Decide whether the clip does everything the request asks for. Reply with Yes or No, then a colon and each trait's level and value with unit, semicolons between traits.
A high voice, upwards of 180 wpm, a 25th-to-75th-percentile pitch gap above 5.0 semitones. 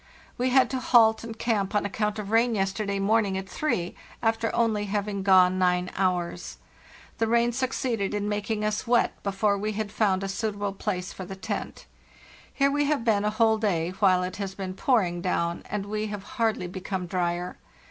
No: high, 205 Hz; average, 190 wpm; average, 2.9 semitones